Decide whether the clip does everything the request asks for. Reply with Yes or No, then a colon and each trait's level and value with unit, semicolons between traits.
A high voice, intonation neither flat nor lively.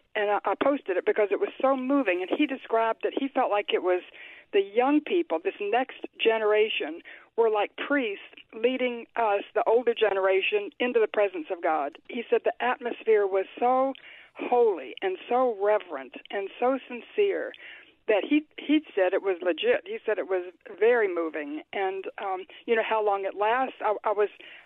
No: high, 245 Hz; wide, 8.2 semitones